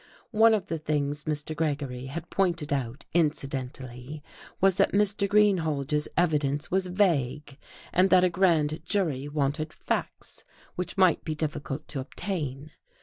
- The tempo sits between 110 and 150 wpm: Yes, average, 140 wpm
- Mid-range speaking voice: Yes, medium, 155 Hz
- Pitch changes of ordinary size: Yes, average, 4.3 semitones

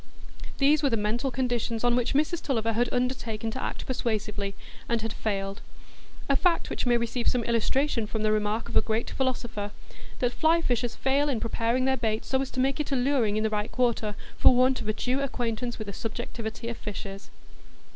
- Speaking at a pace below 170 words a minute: No, average, 200 wpm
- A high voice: Yes, high, 235 Hz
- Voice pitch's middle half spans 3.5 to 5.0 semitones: No, average, 3.0 semitones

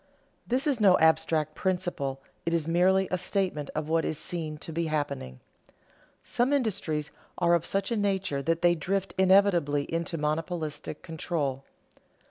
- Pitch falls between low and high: Yes, medium, 165 Hz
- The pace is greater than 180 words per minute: No, average, 155 wpm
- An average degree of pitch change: Yes, average, 3.7 semitones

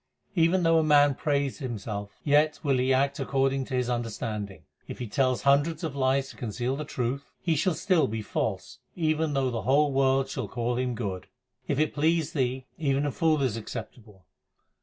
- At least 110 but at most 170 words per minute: No, average, 180 wpm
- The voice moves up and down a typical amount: Yes, average, 3.4 semitones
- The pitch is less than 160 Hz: Yes, low, 135 Hz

